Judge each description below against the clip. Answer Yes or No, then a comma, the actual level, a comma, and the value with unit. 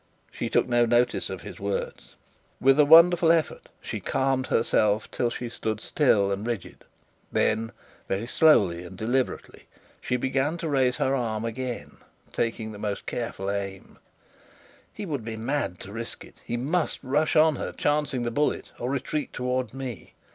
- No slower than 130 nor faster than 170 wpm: Yes, average, 160 wpm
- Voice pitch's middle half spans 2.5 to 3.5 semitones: No, average, 4.2 semitones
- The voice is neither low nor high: No, low, 125 Hz